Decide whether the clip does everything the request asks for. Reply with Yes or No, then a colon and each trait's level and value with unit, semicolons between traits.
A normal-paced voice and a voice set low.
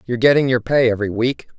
No: fast, 225 wpm; low, 120 Hz